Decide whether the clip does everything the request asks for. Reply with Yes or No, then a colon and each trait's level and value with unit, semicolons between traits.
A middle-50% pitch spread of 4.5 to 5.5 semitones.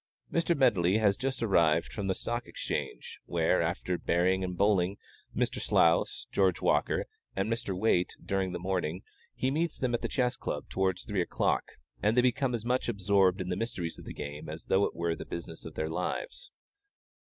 Yes: average, 5.1 semitones